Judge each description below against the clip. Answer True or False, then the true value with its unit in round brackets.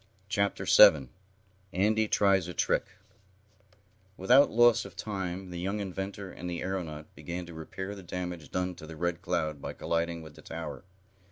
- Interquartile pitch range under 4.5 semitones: True (2.7 semitones)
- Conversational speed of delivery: True (165 wpm)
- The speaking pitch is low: True (90 Hz)